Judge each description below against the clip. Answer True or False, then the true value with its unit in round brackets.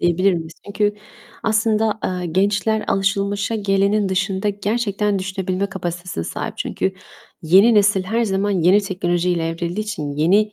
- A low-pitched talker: False (195 Hz)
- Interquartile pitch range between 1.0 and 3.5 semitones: True (2.4 semitones)